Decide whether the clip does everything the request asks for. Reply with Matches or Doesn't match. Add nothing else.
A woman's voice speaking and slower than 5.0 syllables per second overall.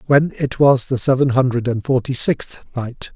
Doesn't match